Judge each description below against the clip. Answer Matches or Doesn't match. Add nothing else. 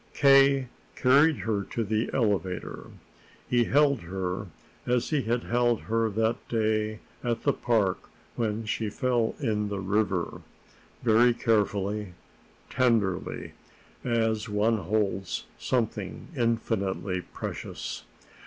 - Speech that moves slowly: Matches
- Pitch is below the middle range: Matches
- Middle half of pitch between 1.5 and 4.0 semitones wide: Matches